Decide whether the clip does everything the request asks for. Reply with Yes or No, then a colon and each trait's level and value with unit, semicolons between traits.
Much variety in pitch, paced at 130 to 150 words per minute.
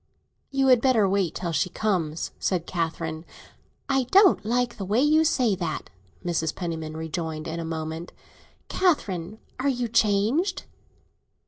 Yes: wide, 7.3 semitones; average, 140 wpm